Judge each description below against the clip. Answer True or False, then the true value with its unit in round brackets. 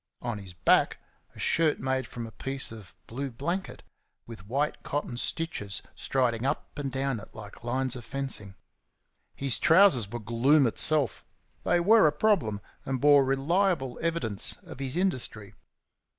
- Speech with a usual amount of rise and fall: True (4.5 semitones)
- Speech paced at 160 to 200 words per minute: False (150 wpm)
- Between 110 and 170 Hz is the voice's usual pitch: True (135 Hz)